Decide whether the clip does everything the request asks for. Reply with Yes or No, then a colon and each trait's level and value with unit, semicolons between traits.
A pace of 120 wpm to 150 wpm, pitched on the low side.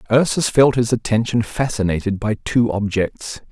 Yes: slow, 135 wpm; low, 110 Hz